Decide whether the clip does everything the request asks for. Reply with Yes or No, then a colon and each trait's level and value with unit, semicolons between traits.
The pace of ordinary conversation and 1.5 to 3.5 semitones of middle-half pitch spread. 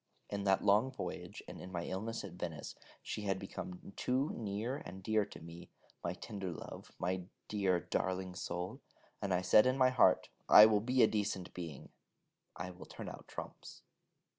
Yes: average, 180 wpm; average, 3.0 semitones